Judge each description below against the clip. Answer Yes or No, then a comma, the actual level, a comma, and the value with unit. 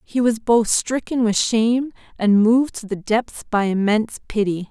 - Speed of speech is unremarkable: Yes, average, 180 wpm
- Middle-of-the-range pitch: No, high, 225 Hz